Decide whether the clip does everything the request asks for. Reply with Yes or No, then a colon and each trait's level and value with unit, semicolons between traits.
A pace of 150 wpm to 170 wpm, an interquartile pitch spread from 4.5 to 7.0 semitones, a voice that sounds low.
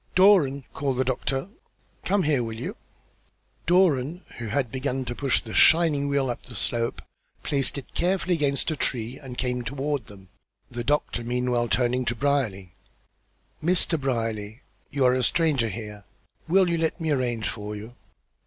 No: average, 160 wpm; average, 3.8 semitones; low, 130 Hz